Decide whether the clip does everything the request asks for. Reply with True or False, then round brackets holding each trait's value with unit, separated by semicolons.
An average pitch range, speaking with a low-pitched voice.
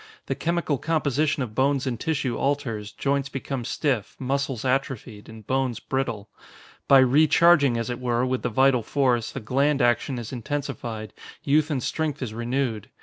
True (3.0 semitones; 130 Hz)